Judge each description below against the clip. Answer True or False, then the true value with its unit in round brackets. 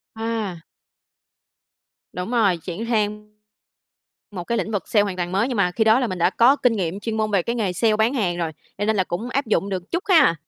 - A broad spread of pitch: False (3.9 semitones)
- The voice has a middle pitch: False (210 Hz)